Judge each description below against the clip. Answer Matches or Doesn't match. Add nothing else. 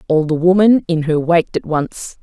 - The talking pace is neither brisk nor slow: Doesn't match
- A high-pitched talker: Doesn't match